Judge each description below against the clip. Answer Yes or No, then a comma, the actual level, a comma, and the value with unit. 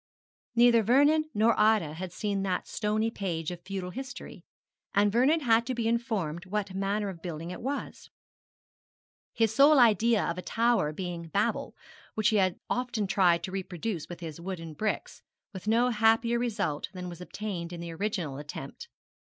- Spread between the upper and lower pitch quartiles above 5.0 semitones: No, average, 4.6 semitones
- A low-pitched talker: No, high, 205 Hz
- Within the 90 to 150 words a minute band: No, average, 165 wpm